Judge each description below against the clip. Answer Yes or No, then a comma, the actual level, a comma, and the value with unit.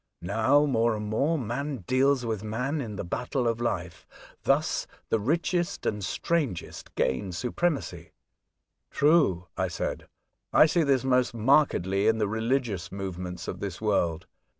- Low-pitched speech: Yes, low, 115 Hz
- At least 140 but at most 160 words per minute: Yes, average, 150 wpm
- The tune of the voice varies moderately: No, wide, 6.0 semitones